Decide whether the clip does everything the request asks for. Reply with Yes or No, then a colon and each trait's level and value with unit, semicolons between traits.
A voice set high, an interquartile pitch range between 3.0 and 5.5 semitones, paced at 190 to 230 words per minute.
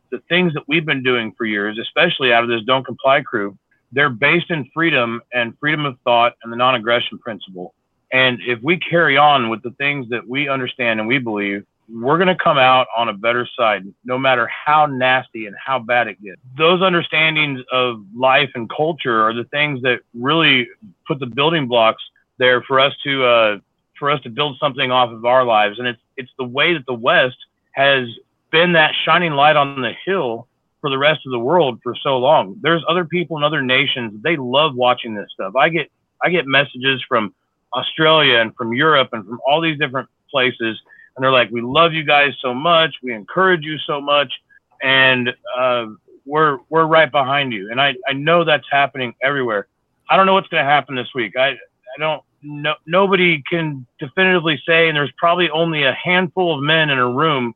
No: low, 135 Hz; average, 4.2 semitones; fast, 205 wpm